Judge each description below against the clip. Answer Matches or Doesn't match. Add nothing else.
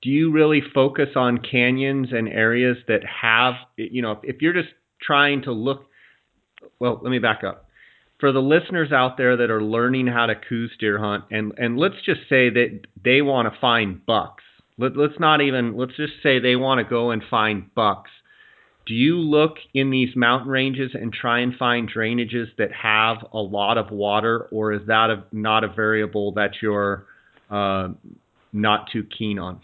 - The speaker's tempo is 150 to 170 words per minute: Doesn't match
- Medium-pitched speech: Doesn't match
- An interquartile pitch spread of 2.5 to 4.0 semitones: Matches